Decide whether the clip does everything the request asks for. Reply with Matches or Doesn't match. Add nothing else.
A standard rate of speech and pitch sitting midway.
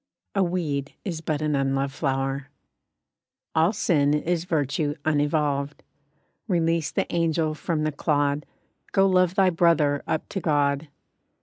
Doesn't match